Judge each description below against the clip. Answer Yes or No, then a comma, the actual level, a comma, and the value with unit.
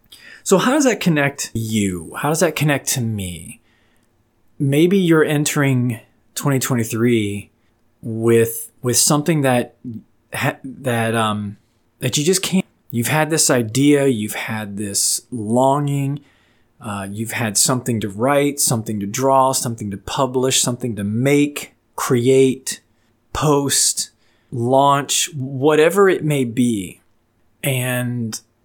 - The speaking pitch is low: Yes, low, 125 Hz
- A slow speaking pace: Yes, slow, 120 wpm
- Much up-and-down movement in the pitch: No, average, 3.8 semitones